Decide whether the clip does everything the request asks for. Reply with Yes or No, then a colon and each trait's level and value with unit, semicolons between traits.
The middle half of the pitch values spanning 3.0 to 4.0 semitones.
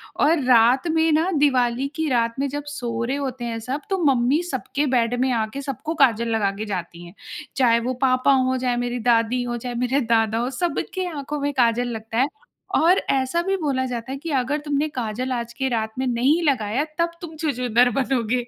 Yes: average, 3.4 semitones